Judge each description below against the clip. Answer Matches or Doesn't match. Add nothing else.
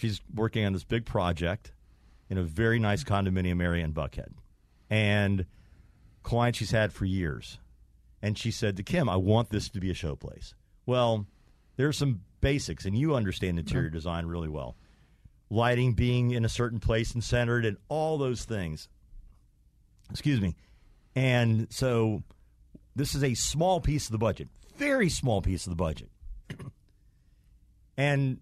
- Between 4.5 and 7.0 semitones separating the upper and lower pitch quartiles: Matches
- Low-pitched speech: Matches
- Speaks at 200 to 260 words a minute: Doesn't match